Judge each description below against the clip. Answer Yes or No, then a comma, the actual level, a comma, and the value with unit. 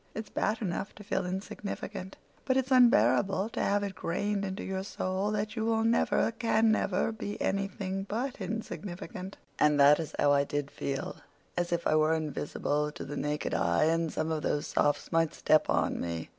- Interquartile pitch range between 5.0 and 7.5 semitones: Yes, wide, 5.4 semitones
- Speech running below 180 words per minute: No, average, 185 wpm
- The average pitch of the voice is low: No, high, 190 Hz